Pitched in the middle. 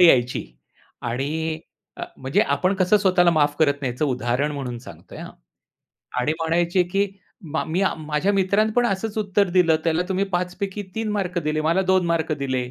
Yes: medium, 170 Hz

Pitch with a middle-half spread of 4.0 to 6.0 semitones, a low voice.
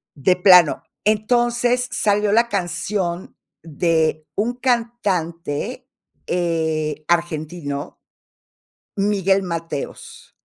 No: average, 4.6 semitones; medium, 180 Hz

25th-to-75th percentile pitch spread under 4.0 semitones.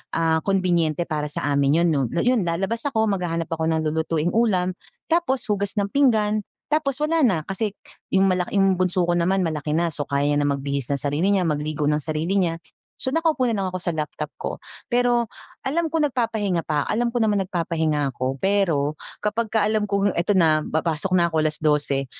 No: wide, 5.4 semitones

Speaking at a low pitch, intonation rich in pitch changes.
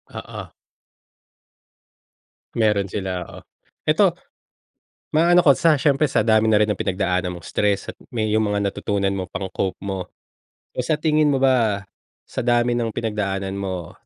No: low, 105 Hz; average, 3.8 semitones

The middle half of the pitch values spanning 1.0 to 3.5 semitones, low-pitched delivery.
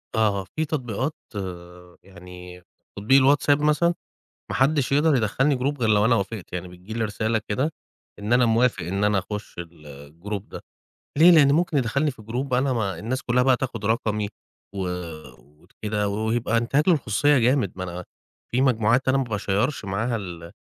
No: average, 4.9 semitones; low, 115 Hz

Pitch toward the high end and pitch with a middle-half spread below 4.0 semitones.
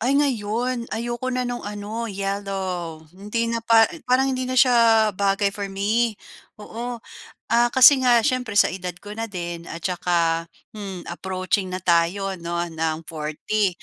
No: high, 205 Hz; average, 4.5 semitones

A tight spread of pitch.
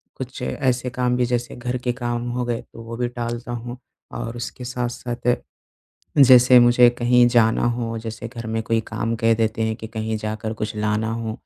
Yes: narrow, 1.5 semitones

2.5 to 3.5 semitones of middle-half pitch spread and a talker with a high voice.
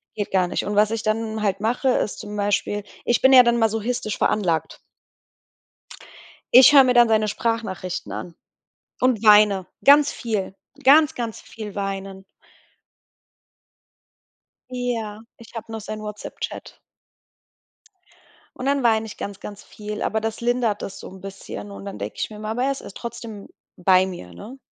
Yes: average, 3.0 semitones; high, 215 Hz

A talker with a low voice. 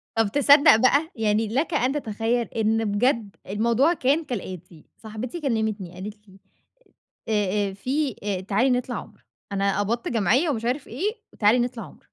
No: high, 225 Hz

